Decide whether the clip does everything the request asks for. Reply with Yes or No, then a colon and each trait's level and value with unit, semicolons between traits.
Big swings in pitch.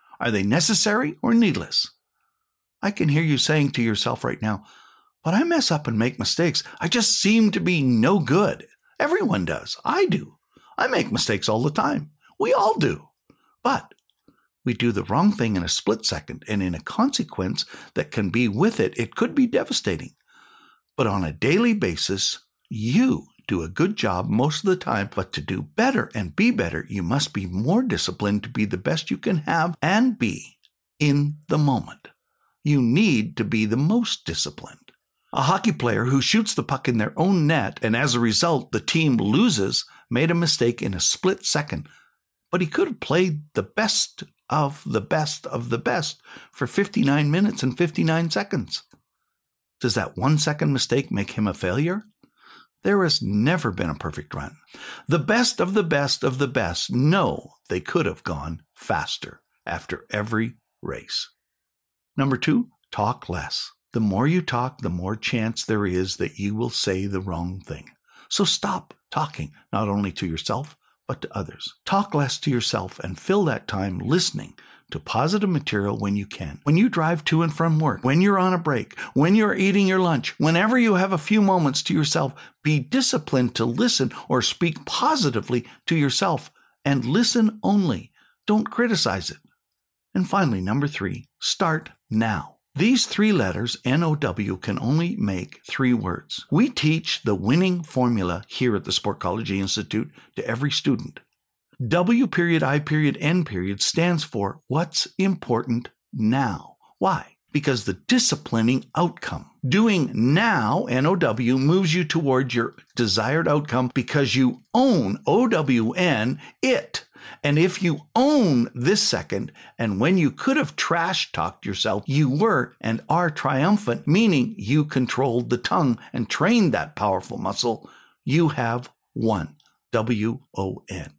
Yes: wide, 8.0 semitones